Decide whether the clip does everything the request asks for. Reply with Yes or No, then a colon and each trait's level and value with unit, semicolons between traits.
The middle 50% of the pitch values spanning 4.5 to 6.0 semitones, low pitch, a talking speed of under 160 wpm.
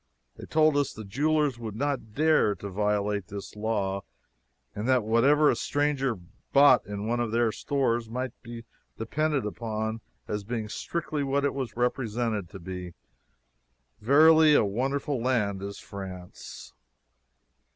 Yes: average, 5.2 semitones; low, 115 Hz; average, 140 wpm